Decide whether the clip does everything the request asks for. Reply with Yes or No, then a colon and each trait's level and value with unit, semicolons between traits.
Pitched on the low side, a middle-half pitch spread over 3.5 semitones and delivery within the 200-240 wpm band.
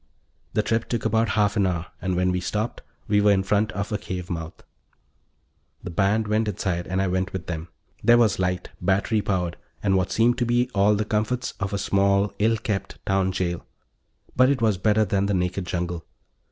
No: low, 100 Hz; average, 2.7 semitones; fast, 205 wpm